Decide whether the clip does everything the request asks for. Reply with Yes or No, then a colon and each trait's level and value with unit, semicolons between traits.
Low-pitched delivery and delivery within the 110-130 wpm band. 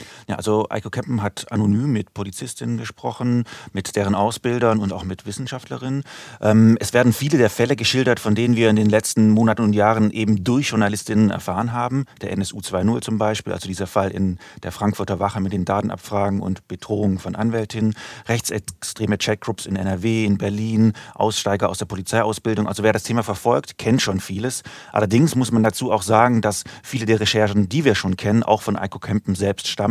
No: low, 110 Hz; average, 185 wpm